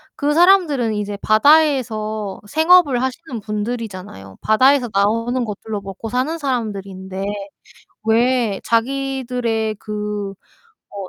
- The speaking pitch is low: No, high, 225 Hz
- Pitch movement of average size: Yes, average, 4.3 semitones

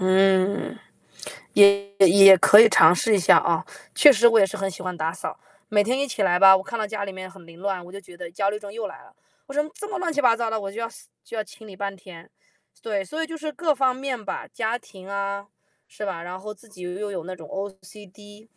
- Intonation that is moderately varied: Yes, average, 3.0 semitones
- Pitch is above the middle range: Yes, high, 200 Hz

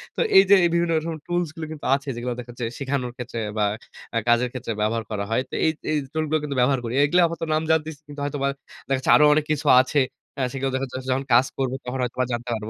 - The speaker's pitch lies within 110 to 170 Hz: Yes, low, 135 Hz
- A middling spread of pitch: Yes, average, 3.9 semitones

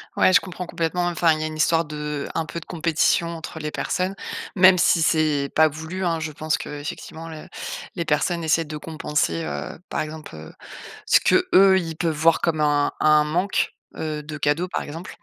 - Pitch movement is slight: Yes, narrow, 1.9 semitones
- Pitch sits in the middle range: Yes, medium, 160 Hz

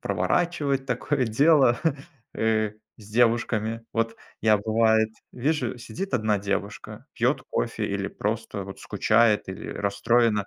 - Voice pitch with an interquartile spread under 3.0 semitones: Yes, narrow, 2.5 semitones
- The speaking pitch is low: Yes, low, 115 Hz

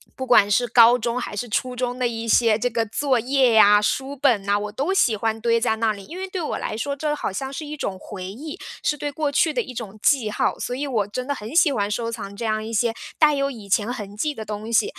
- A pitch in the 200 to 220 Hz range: No, high, 235 Hz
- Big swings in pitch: No, average, 4.3 semitones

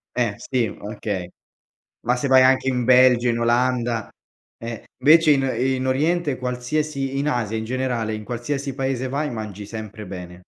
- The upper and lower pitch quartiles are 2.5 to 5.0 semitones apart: Yes, average, 2.9 semitones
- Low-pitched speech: Yes, low, 125 Hz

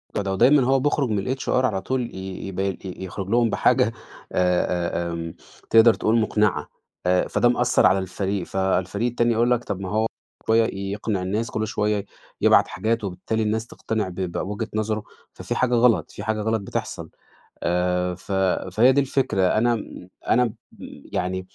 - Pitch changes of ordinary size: Yes, average, 3.5 semitones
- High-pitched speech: No, low, 105 Hz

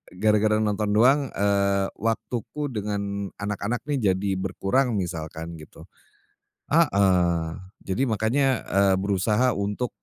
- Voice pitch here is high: No, low, 100 Hz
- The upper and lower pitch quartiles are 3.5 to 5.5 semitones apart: No, average, 2.7 semitones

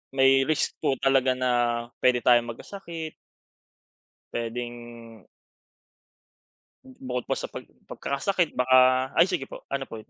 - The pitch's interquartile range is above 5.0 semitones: No, narrow, 2.4 semitones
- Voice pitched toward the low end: Yes, low, 130 Hz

